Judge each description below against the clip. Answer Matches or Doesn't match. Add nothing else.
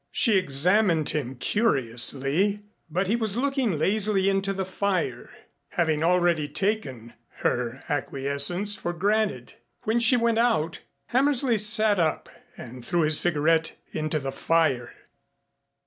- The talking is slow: Matches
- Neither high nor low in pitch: Matches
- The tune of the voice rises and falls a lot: Matches